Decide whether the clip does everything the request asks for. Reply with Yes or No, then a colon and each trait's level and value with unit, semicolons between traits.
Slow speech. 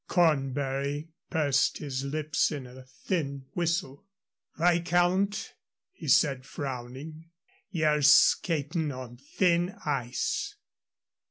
Yes: slow, 90 wpm